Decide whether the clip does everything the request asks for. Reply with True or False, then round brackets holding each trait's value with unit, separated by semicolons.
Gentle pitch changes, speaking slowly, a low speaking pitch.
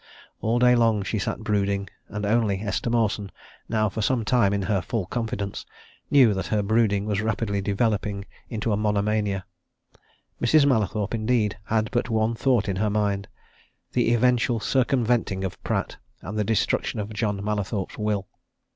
False (2.3 semitones; 160 wpm; 105 Hz)